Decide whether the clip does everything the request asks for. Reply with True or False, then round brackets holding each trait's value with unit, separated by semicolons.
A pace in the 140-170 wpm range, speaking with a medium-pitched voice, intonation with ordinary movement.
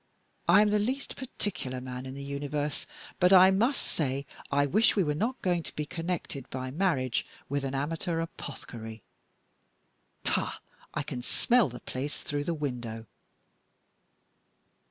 False (150 wpm; 145 Hz; 5.9 semitones)